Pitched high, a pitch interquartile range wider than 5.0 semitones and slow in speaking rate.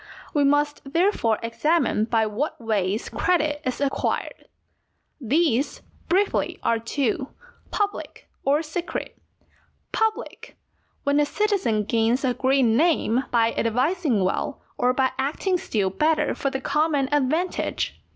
Yes: very high, 275 Hz; wide, 5.5 semitones; slow, 120 wpm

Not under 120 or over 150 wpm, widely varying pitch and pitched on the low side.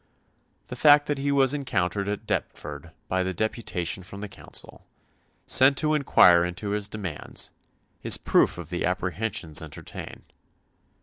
Yes: average, 140 wpm; wide, 7.0 semitones; low, 100 Hz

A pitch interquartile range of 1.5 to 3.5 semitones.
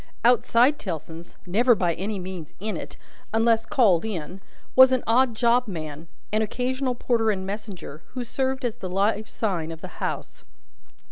No: average, 5.0 semitones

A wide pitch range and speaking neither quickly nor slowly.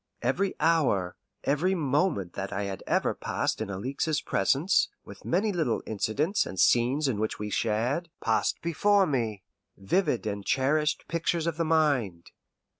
Yes: wide, 7.7 semitones; average, 150 wpm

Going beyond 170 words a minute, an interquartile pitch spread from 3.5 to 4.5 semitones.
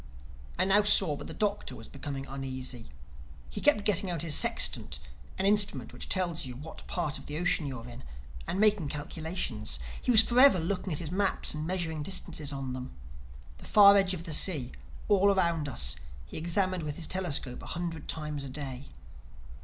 No: average, 190 wpm; average, 5.1 semitones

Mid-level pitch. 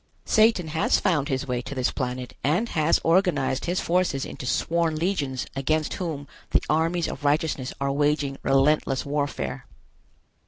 Yes: medium, 150 Hz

